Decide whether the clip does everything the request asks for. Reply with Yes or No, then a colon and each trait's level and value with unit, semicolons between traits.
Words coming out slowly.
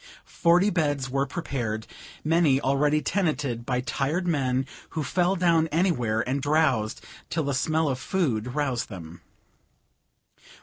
Yes: slow, 130 wpm